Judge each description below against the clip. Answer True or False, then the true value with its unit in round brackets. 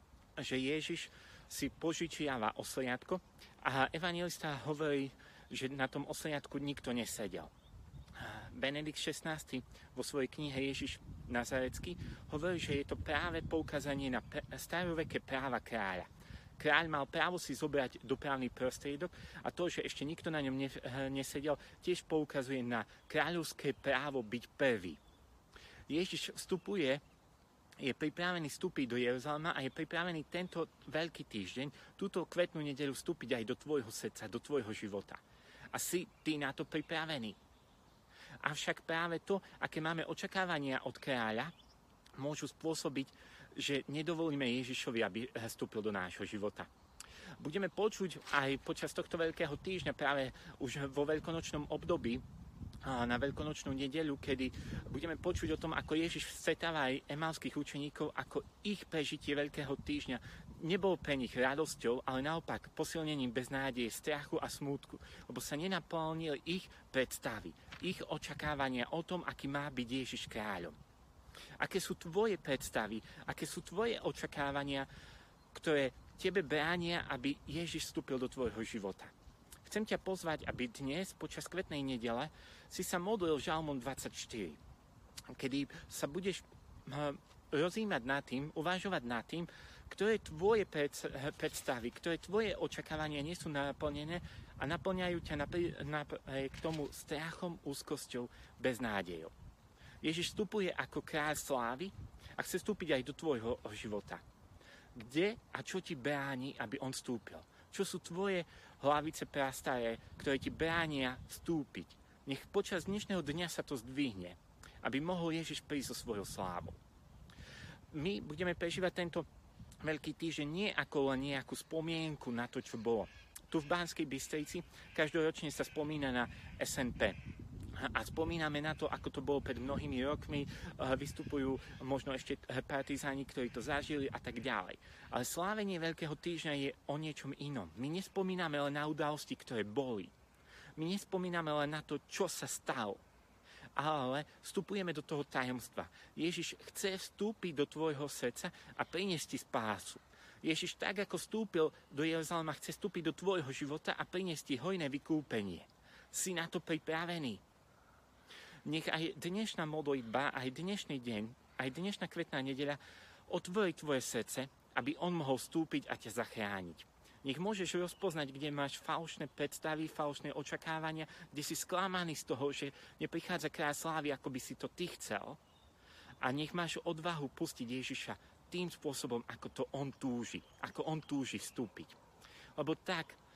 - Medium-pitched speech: True (150 Hz)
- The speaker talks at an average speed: True (140 wpm)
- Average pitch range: True (3.8 semitones)